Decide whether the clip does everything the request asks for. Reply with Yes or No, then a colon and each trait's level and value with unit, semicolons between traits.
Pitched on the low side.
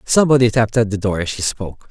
Yes: low, 110 Hz